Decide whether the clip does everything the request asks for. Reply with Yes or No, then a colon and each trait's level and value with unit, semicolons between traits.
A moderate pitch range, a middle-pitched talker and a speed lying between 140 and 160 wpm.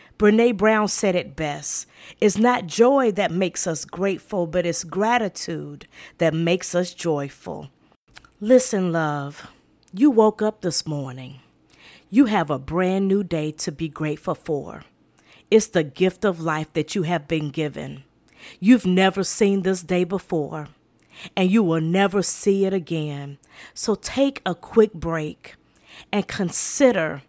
Yes: average, 4.7 semitones; medium, 180 Hz; average, 145 wpm